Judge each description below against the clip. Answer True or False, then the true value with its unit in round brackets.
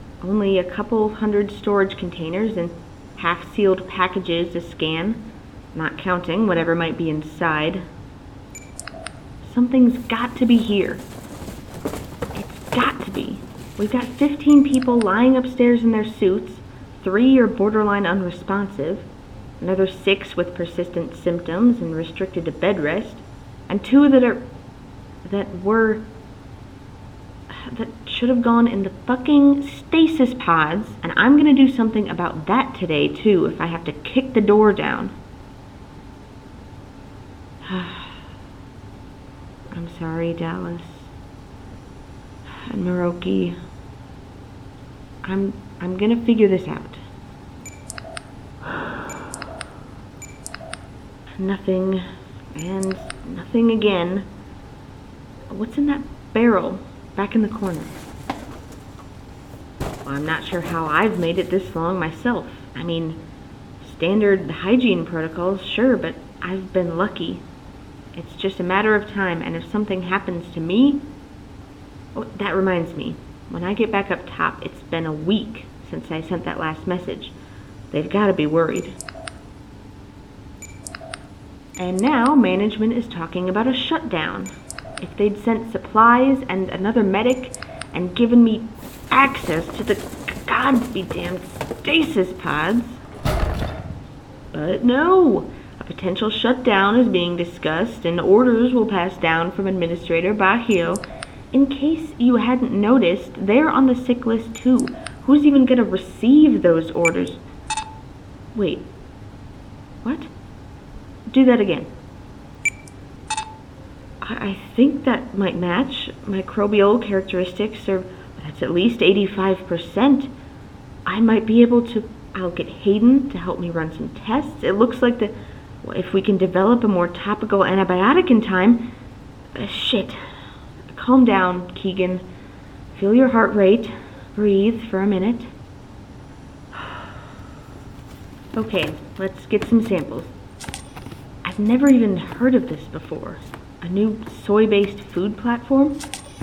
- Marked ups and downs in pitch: True (5.8 semitones)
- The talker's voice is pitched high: True (195 Hz)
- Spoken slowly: True (120 wpm)